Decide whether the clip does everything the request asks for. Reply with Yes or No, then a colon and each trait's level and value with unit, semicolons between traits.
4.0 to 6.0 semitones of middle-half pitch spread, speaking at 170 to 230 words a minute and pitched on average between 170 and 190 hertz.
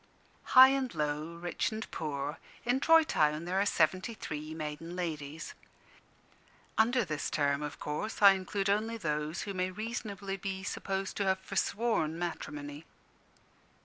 No: wide, 5.4 semitones; average, 145 wpm; medium, 185 Hz